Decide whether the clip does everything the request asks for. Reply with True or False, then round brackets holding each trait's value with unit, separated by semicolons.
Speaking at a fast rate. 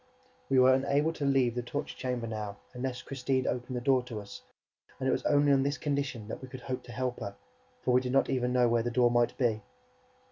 True (240 wpm)